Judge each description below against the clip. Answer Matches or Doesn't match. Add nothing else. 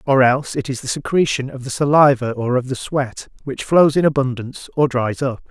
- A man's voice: Matches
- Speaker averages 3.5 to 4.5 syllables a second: Doesn't match